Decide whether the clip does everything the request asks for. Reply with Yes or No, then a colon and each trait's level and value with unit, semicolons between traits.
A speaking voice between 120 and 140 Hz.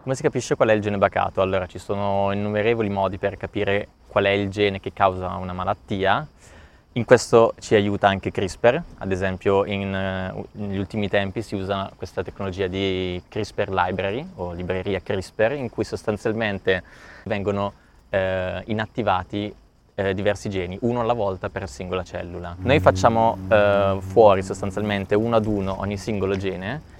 No: low, 100 Hz